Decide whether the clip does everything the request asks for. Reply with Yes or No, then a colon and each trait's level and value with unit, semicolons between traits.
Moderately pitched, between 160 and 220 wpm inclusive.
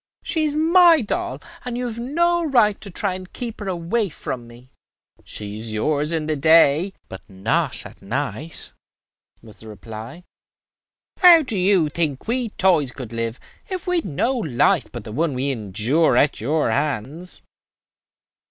Yes: medium, 160 Hz; average, 165 wpm